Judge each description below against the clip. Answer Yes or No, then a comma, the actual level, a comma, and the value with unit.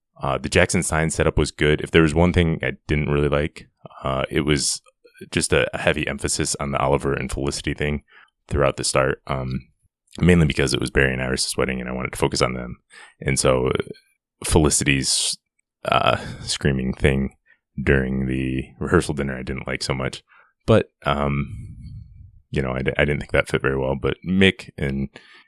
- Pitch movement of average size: No, narrow, 2.3 semitones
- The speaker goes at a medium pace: Yes, average, 185 wpm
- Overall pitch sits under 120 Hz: Yes, very low, 70 Hz